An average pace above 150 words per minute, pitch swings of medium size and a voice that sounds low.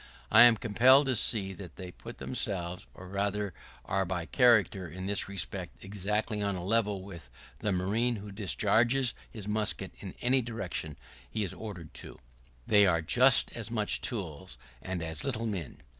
Yes: average, 170 wpm; average, 3.6 semitones; low, 100 Hz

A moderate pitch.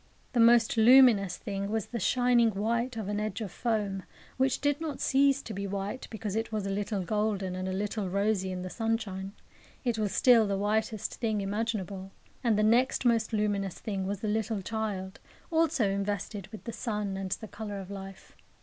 No: high, 210 Hz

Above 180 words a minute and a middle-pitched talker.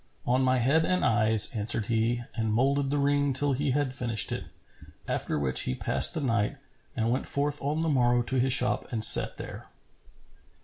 No: average, 190 wpm; low, 125 Hz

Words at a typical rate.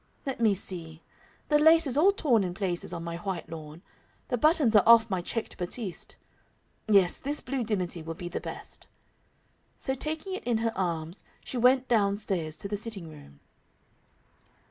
Yes: average, 175 wpm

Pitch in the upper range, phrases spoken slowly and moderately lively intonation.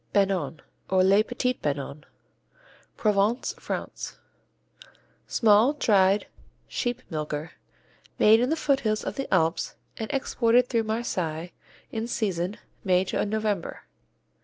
Yes: high, 210 Hz; slow, 110 wpm; average, 4.3 semitones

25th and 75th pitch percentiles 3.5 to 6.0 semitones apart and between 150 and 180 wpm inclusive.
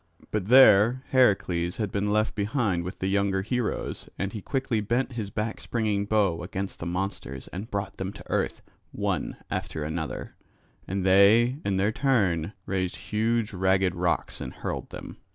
No: average, 2.8 semitones; average, 165 wpm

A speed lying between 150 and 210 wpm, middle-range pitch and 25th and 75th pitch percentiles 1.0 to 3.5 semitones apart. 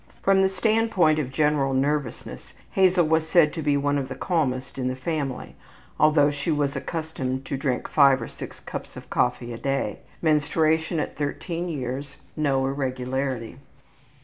Yes: average, 160 wpm; medium, 145 Hz; average, 3.1 semitones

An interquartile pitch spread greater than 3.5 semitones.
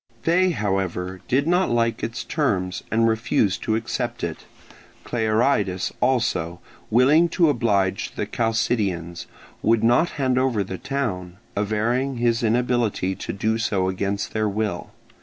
Yes: average, 4.2 semitones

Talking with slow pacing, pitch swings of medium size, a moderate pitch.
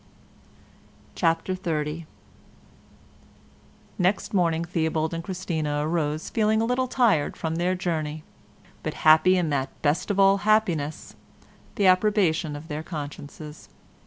Yes: slow, 120 wpm; average, 3.3 semitones; medium, 165 Hz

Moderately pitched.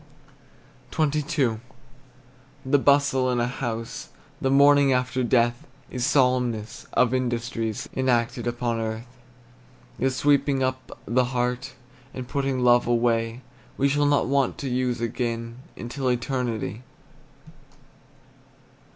No: low, 125 Hz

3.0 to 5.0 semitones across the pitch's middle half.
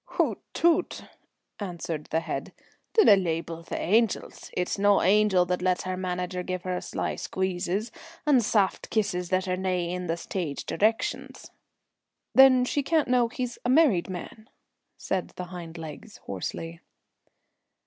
Yes: average, 3.7 semitones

